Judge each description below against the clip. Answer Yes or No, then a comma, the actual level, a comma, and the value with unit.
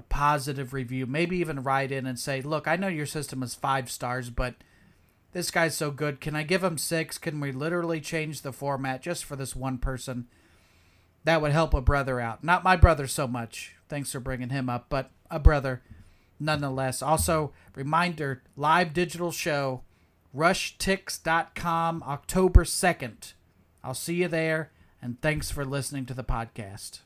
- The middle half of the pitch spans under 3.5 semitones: No, average, 3.9 semitones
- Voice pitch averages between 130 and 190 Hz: Yes, medium, 140 Hz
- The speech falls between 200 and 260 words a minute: No, average, 170 wpm